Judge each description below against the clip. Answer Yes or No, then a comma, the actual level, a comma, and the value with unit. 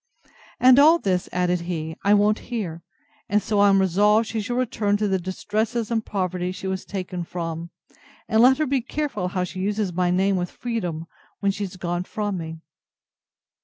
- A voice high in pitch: Yes, high, 195 Hz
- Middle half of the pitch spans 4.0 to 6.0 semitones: No, average, 3.3 semitones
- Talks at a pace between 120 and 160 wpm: No, average, 190 wpm